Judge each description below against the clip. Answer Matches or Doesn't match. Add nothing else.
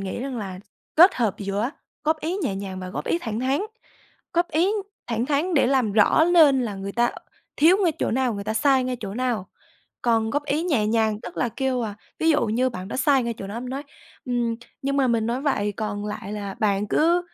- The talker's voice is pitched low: Doesn't match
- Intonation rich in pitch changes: Doesn't match